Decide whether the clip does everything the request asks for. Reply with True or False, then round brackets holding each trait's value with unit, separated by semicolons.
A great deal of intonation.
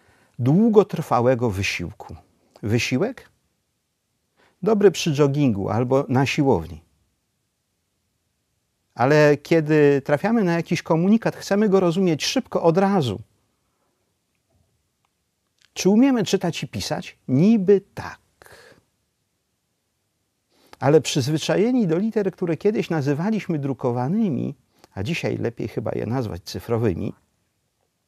True (7.9 semitones)